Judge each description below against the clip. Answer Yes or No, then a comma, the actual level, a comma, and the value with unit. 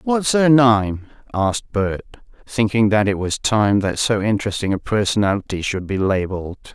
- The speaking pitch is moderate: No, low, 105 Hz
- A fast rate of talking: No, average, 160 wpm